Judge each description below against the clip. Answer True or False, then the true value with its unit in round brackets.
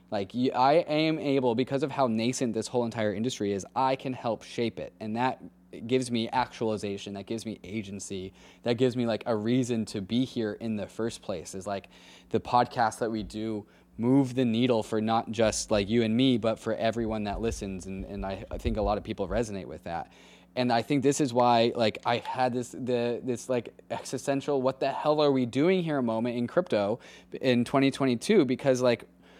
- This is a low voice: True (115 Hz)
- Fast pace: True (210 wpm)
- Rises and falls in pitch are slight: False (3.5 semitones)